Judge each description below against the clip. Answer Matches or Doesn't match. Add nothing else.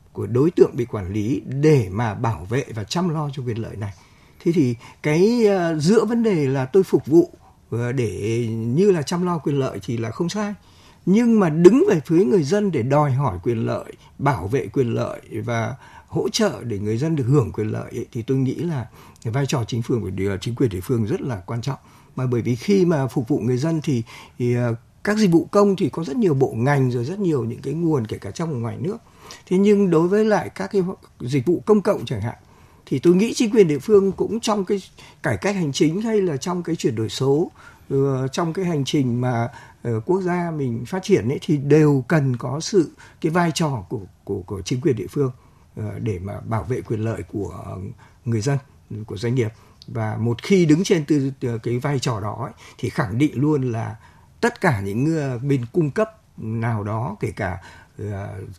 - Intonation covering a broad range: Matches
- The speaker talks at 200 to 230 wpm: Matches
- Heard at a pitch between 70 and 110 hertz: Doesn't match